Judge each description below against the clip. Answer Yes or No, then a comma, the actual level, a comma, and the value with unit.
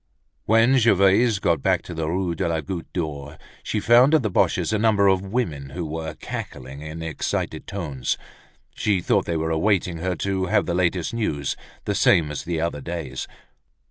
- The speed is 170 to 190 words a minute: Yes, average, 185 wpm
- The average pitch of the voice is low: Yes, very low, 85 Hz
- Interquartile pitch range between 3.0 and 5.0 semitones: Yes, average, 3.9 semitones